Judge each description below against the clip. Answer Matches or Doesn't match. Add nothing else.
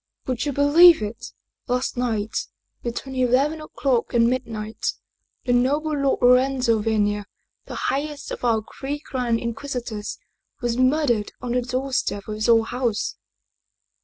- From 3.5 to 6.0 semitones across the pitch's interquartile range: Doesn't match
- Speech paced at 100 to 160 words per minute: Matches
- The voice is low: Doesn't match